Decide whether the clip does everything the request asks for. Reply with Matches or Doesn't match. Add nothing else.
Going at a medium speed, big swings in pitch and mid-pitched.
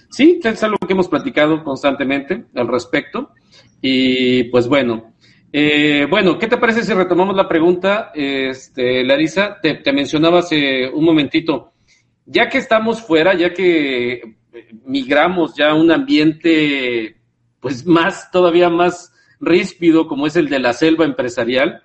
Matches